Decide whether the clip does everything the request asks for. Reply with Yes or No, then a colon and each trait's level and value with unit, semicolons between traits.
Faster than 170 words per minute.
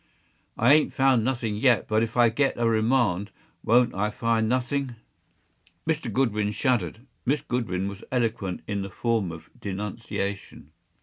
No: average, 145 wpm